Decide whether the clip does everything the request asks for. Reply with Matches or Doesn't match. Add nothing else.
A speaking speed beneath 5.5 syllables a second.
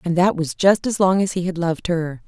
Doesn't match